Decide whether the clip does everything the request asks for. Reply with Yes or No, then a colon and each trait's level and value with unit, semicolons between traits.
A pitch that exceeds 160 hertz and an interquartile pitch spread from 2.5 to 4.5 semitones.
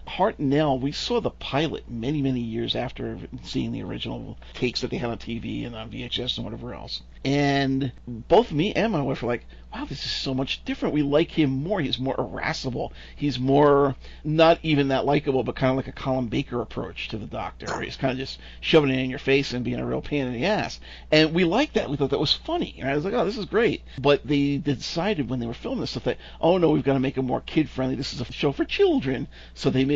No: low, 135 Hz; average, 2.9 semitones